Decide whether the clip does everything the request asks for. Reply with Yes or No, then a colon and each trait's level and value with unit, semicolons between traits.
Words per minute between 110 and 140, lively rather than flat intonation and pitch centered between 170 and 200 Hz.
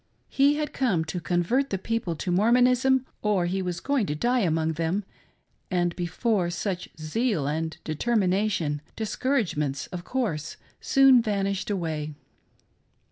Yes: slow, 135 wpm; wide, 6.5 semitones; high, 190 Hz